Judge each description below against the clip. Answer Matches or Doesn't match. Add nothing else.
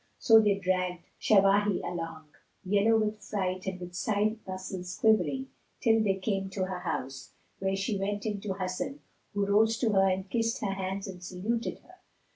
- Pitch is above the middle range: Matches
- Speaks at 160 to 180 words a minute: Matches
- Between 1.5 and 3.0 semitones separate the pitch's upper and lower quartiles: Matches